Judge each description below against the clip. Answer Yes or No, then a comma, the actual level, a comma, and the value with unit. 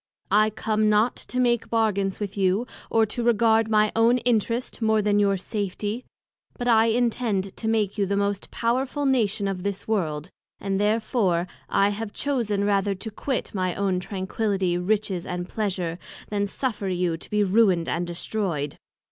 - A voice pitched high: Yes, high, 205 Hz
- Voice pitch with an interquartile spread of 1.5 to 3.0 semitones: Yes, average, 2.7 semitones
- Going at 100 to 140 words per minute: No, average, 165 wpm